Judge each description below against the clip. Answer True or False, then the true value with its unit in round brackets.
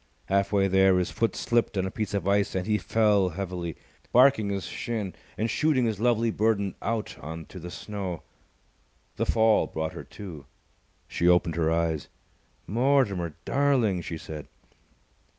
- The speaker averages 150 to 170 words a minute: True (160 wpm)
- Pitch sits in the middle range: False (100 Hz)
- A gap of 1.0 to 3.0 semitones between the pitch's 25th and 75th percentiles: False (4.1 semitones)